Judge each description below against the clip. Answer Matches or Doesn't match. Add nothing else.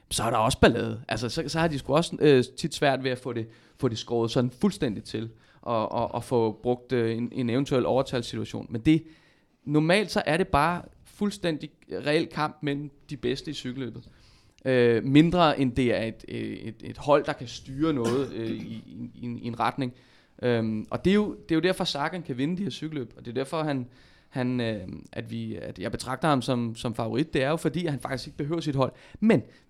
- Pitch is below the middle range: Matches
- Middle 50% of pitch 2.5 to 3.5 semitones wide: Doesn't match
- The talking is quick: Matches